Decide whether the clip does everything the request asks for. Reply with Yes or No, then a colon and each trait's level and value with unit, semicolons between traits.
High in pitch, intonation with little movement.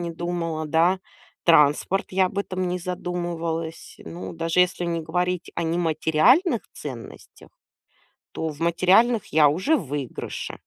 No: medium, 170 Hz; narrow, 2.1 semitones